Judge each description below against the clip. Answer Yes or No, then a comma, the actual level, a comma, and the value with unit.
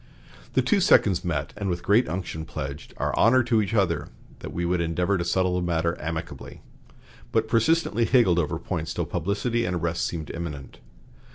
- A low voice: Yes, very low, 90 Hz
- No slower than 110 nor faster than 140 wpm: No, average, 180 wpm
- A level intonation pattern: No, average, 4.0 semitones